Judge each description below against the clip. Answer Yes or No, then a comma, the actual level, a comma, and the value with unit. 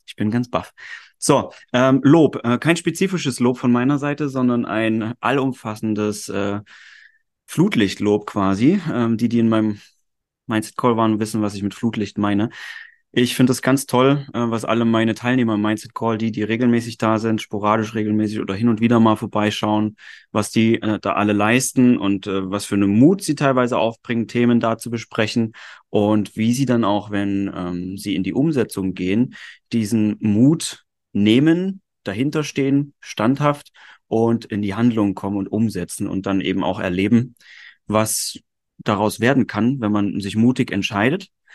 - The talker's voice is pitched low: Yes, low, 110 Hz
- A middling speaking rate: Yes, average, 170 wpm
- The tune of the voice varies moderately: Yes, average, 3.1 semitones